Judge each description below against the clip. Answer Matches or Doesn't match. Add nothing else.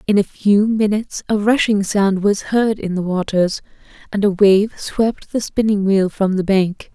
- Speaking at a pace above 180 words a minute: Matches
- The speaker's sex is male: Doesn't match